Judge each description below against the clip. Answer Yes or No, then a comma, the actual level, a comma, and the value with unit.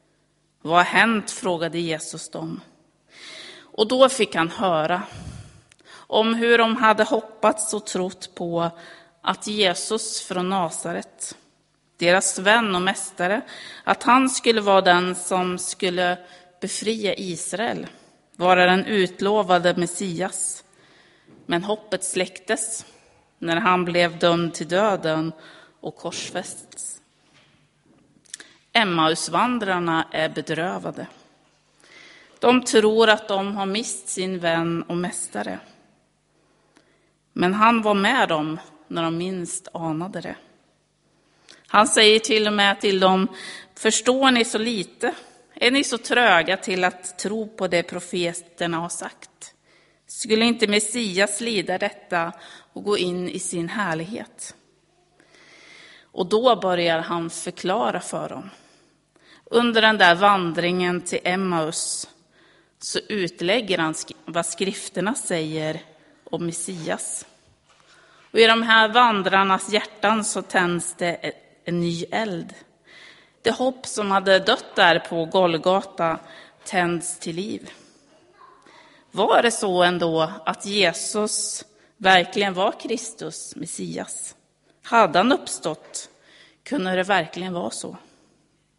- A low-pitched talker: No, medium, 185 Hz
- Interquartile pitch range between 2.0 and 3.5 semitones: No, average, 3.9 semitones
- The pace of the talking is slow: Yes, slow, 115 wpm